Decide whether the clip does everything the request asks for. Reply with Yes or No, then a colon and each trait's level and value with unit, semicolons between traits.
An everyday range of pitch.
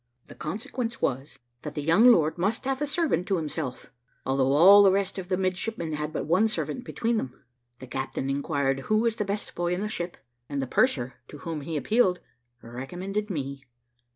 No: wide, 6.9 semitones